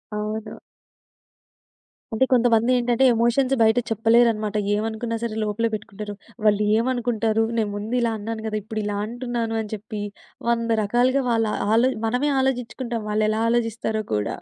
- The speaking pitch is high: Yes, high, 225 Hz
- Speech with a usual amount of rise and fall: No, narrow, 1.8 semitones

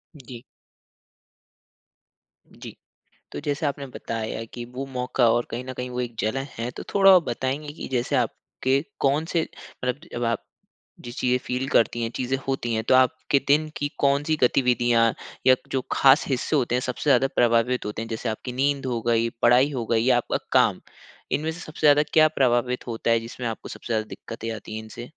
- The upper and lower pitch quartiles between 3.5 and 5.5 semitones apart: No, average, 2.8 semitones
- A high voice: No, low, 125 Hz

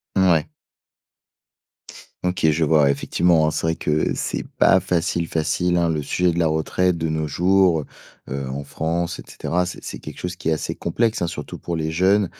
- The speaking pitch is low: Yes, very low, 85 Hz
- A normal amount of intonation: No, narrow, 2.3 semitones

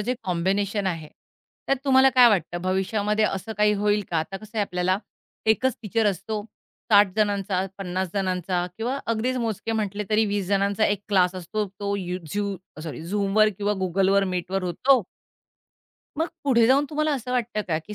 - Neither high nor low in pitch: No, high, 205 Hz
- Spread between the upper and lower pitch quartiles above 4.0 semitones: No, average, 2.8 semitones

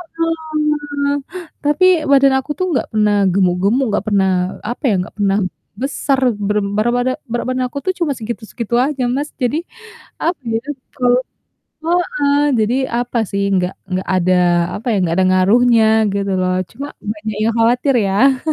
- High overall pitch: Yes, high, 240 Hz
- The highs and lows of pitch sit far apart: Yes, wide, 6.0 semitones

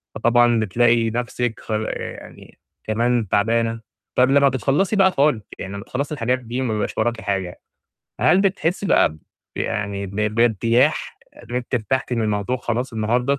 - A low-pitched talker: Yes, low, 120 Hz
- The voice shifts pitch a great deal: No, average, 2.9 semitones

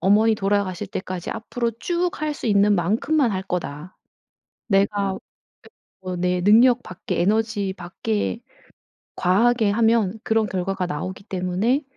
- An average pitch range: Yes, average, 3.5 semitones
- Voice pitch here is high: Yes, high, 200 Hz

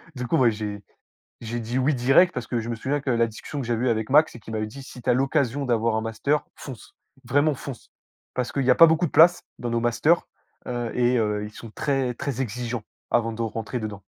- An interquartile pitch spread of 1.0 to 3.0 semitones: No, average, 3.4 semitones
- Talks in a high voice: No, low, 120 Hz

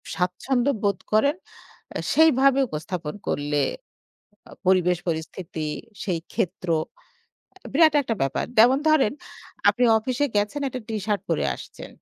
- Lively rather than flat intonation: Yes, wide, 7.0 semitones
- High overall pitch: Yes, high, 210 Hz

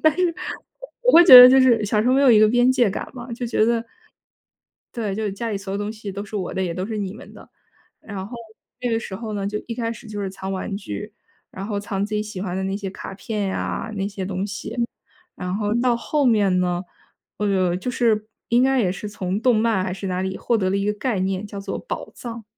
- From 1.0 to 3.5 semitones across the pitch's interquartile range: Yes, average, 3.2 semitones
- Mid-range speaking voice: No, high, 210 Hz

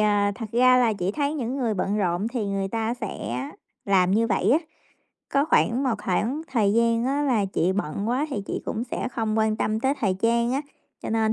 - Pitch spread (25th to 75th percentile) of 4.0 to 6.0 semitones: No, average, 3.5 semitones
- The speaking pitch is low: No, high, 225 Hz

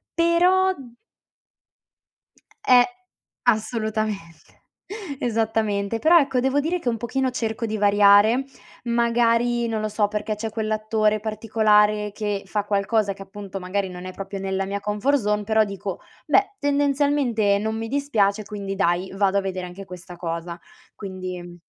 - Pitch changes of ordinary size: Yes, average, 3.0 semitones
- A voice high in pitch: Yes, high, 215 Hz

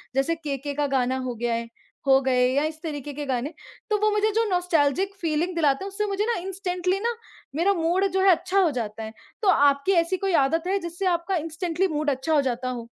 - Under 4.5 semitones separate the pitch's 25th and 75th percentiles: No, wide, 5.6 semitones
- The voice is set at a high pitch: Yes, very high, 325 Hz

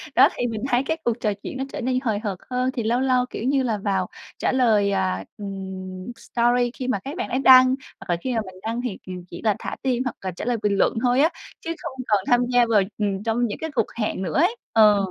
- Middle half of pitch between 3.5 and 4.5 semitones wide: Yes, average, 4.0 semitones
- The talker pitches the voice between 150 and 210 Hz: No, high, 230 Hz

